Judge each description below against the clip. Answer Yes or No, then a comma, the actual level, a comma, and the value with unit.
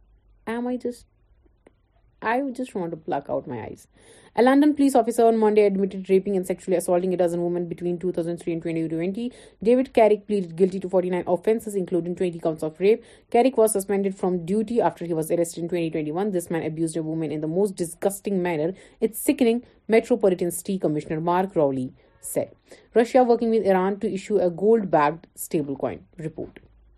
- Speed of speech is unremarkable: Yes, average, 150 wpm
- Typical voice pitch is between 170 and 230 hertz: Yes, medium, 185 Hz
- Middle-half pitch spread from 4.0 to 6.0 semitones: Yes, average, 4.6 semitones